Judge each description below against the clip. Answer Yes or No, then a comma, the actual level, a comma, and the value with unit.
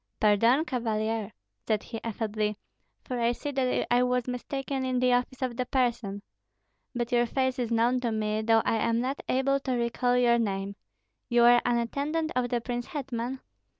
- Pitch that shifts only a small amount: Yes, narrow, 1.9 semitones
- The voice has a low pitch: No, high, 240 Hz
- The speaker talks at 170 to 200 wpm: Yes, average, 185 wpm